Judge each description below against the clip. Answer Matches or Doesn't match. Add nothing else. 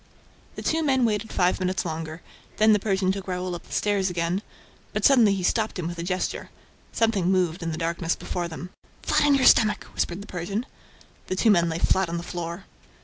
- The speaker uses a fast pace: Matches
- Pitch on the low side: Doesn't match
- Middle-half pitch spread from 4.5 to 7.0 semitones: Doesn't match